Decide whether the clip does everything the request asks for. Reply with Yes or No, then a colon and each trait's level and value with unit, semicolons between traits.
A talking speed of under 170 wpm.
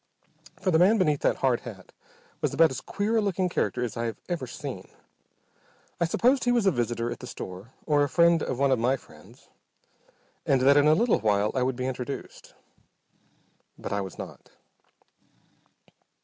No: average, 185 wpm